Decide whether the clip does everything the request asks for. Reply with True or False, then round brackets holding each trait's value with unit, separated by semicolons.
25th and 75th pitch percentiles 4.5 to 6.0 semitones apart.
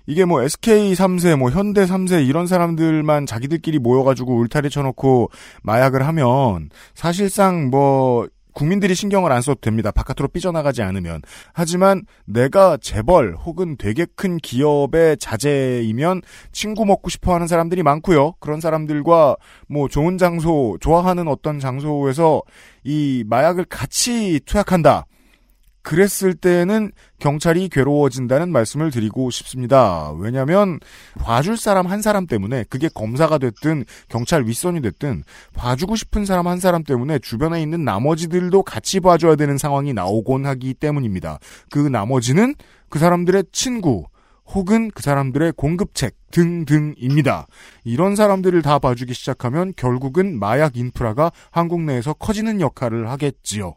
True (5.4 semitones)